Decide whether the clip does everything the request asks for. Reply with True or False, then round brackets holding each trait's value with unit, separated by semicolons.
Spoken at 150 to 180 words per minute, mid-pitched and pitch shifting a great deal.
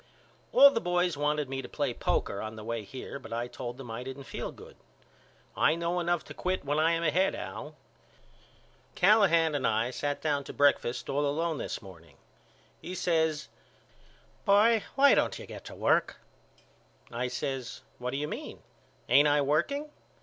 True (175 wpm; 145 Hz; 5.7 semitones)